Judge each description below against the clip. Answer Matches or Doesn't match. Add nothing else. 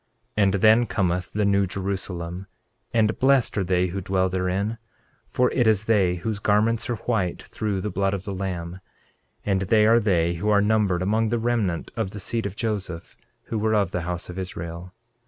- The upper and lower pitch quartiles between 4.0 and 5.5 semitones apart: Doesn't match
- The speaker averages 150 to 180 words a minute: Doesn't match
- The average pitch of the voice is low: Matches